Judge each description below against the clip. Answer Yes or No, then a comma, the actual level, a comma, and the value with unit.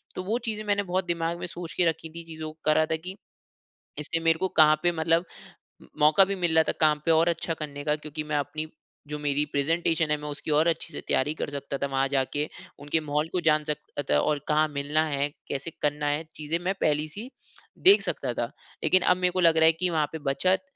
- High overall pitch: No, medium, 155 Hz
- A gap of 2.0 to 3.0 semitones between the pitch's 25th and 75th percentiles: Yes, narrow, 2.4 semitones